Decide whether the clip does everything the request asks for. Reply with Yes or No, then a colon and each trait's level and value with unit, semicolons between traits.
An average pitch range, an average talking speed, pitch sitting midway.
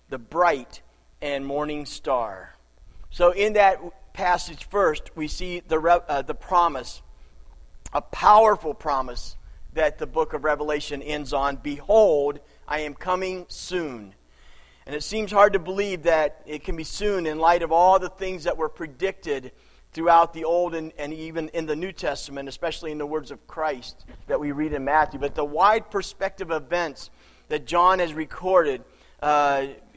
Yes: average, 4.1 semitones; average, 165 wpm; medium, 155 Hz